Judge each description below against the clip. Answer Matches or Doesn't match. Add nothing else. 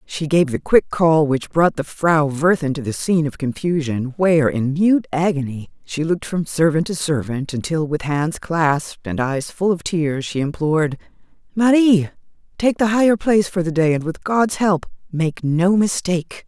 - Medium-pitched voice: Matches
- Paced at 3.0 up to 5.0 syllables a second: Matches